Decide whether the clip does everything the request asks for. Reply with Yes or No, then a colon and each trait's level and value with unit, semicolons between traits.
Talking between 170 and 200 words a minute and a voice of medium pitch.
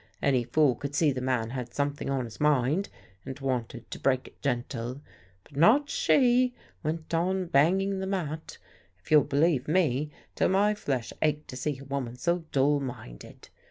Yes: average, 175 wpm; medium, 145 Hz